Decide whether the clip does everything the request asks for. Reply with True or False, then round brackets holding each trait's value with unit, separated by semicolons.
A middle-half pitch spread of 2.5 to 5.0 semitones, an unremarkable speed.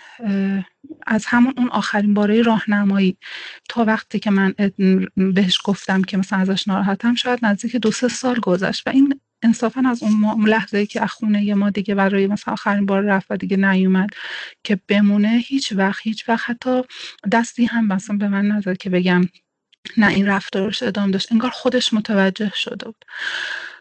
False (3.1 semitones; 170 wpm)